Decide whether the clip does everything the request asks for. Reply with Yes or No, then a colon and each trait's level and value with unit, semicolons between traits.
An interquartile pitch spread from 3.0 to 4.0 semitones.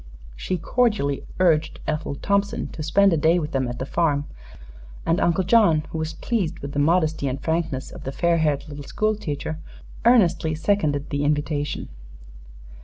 Yes: average, 3.7 semitones